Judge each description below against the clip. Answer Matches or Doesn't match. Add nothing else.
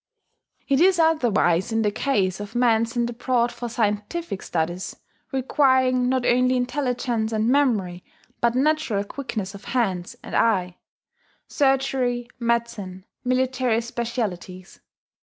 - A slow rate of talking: Matches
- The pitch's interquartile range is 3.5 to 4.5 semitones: Matches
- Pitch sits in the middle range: Doesn't match